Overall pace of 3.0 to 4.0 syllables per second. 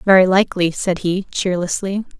No: 5.1 syllables/s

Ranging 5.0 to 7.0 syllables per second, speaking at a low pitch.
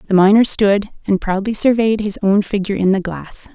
No: 5.4 syllables/s; high, 200 Hz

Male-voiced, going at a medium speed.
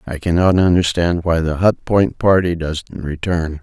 Yes: male; average, 165 wpm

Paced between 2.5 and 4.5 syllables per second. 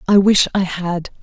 Yes: 4.3 syllables/s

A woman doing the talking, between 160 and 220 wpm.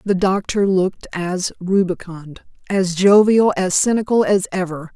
No: female; slow, 135 wpm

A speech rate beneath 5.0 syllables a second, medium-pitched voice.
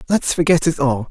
No: 5.6 syllables/s; medium, 155 Hz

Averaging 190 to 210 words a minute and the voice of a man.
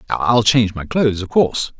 Yes: average, 200 wpm; male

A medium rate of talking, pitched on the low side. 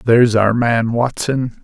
Yes: average, 145 wpm; low, 120 Hz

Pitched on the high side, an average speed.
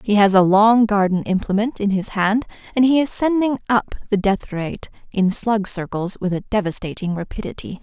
Yes: high, 205 Hz; average, 185 wpm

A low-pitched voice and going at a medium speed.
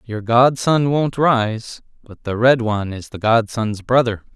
Yes: low, 115 Hz; average, 165 wpm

